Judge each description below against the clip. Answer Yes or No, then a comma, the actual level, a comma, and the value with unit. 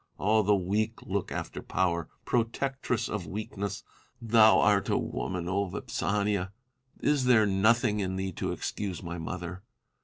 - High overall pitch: No, low, 100 Hz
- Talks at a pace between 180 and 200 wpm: No, average, 140 wpm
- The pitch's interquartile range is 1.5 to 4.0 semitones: Yes, average, 2.8 semitones